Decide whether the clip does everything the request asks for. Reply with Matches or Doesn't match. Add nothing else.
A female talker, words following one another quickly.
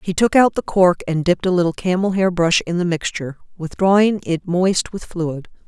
Matches